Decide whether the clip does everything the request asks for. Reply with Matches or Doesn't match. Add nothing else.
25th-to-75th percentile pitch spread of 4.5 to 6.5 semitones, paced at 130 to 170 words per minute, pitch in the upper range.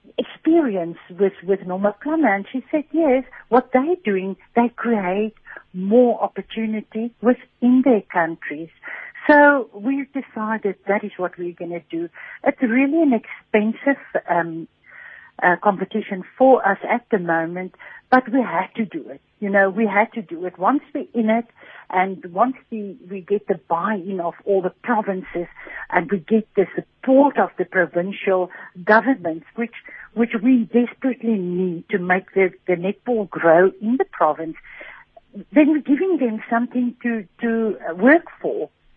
Matches